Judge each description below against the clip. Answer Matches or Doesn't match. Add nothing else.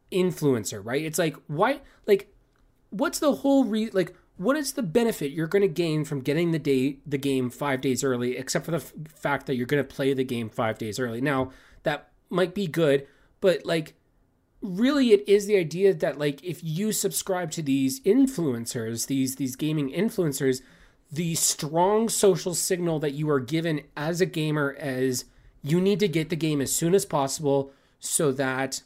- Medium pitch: Matches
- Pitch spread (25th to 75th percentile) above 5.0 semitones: Matches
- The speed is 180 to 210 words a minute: Matches